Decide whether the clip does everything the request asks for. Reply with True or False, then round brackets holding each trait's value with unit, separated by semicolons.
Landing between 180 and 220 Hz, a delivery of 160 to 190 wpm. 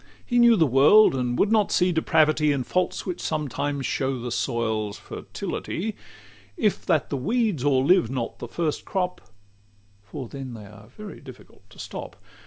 False (145 Hz; 165 wpm)